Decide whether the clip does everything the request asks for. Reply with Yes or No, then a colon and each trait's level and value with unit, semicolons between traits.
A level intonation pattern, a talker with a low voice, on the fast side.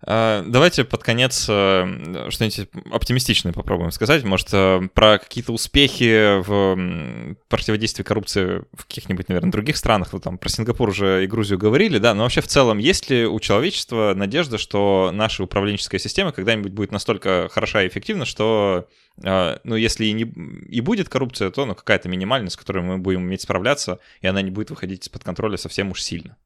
No: average, 3.2 semitones; low, 105 Hz; fast, 170 wpm